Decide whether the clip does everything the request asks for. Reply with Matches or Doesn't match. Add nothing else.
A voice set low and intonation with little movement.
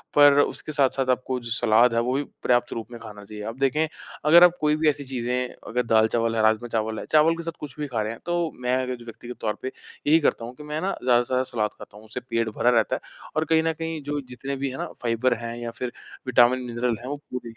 Doesn't match